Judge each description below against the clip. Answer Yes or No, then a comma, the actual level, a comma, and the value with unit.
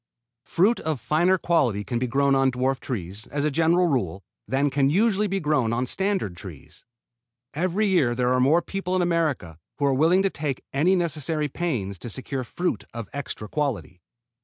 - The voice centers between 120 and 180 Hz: Yes, medium, 140 Hz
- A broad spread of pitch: Yes, wide, 5.8 semitones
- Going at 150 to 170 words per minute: No, average, 185 wpm